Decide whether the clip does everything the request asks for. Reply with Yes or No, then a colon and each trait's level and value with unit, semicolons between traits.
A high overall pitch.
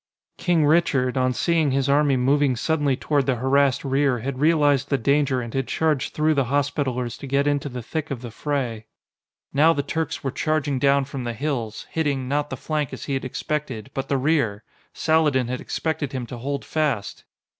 No: medium, 140 Hz